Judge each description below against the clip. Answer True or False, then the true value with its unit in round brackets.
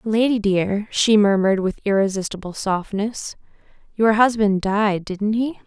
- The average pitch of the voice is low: False (205 Hz)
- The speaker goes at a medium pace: False (125 wpm)